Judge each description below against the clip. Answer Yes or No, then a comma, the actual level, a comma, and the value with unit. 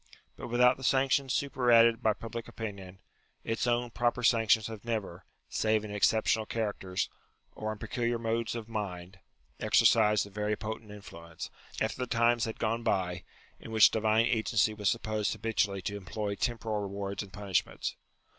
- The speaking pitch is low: Yes, low, 110 Hz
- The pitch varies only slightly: Yes, narrow, 2.3 semitones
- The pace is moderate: Yes, average, 160 wpm